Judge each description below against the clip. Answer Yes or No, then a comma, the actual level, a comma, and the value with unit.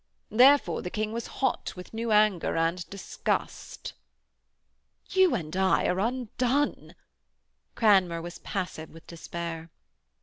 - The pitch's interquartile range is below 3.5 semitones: No, average, 5.3 semitones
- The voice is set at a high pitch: Yes, high, 195 Hz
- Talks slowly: Yes, slow, 115 wpm